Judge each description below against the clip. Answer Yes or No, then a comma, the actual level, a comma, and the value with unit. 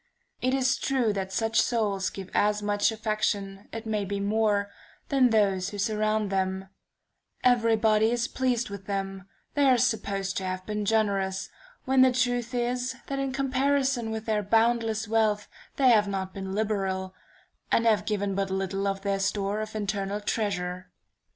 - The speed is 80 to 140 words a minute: No, average, 165 wpm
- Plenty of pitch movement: No, average, 2.9 semitones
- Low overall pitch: No, high, 210 Hz